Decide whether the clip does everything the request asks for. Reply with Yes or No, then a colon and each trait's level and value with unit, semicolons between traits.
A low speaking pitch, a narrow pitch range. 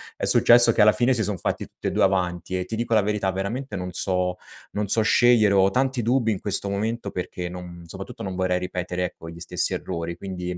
No: very low, 95 Hz; average, 3.4 semitones